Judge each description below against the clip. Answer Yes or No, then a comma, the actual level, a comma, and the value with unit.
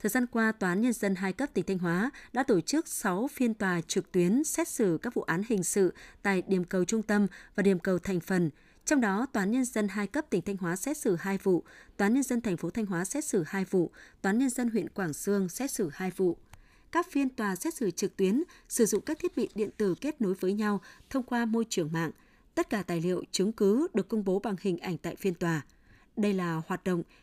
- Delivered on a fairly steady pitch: No, average, 4.3 semitones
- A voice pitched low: No, high, 200 Hz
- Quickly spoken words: Yes, fast, 260 wpm